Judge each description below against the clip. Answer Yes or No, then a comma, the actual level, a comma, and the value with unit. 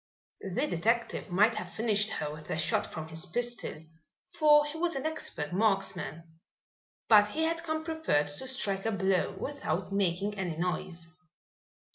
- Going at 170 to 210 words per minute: No, average, 155 wpm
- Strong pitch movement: Yes, wide, 7.5 semitones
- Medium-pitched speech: No, high, 205 Hz